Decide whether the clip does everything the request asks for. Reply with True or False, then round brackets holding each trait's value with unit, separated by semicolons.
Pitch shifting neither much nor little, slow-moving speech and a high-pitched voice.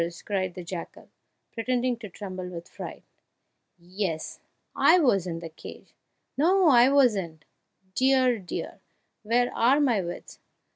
False (6.1 semitones; 130 wpm; 210 Hz)